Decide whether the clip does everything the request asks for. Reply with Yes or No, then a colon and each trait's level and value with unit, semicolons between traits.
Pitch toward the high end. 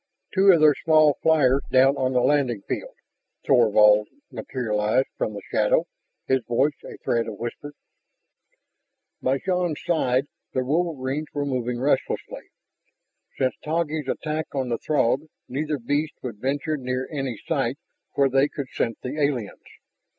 No: low, 135 Hz